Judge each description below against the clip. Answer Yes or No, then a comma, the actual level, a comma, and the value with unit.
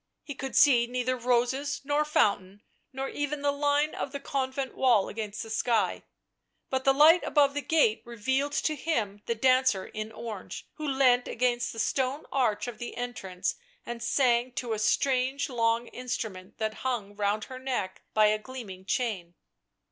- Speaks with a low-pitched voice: No, high, 245 Hz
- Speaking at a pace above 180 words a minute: No, average, 170 wpm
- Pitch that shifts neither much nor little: Yes, average, 3.8 semitones